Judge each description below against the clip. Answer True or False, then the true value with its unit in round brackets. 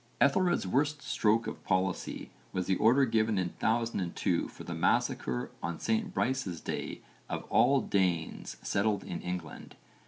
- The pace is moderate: True (145 wpm)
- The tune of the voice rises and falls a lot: True (6.4 semitones)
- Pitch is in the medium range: False (105 Hz)